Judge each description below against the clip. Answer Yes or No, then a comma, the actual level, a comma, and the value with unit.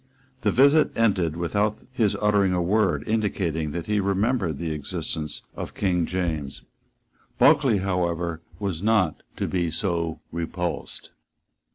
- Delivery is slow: Yes, slow, 130 wpm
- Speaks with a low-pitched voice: Yes, very low, 90 Hz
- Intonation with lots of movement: No, average, 3.9 semitones